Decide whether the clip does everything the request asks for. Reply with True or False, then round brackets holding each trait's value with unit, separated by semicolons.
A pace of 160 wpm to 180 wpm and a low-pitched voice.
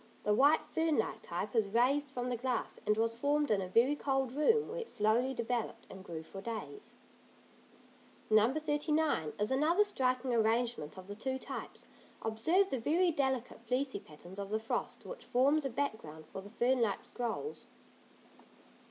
False (170 wpm; 245 Hz)